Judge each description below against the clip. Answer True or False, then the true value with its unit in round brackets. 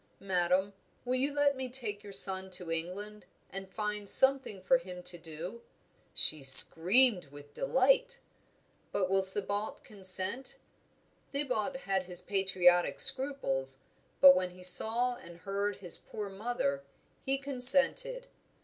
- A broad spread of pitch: True (5.8 semitones)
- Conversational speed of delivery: False (130 wpm)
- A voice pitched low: False (200 Hz)